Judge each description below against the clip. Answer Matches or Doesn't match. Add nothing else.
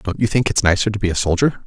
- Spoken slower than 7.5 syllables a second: Matches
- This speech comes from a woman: Doesn't match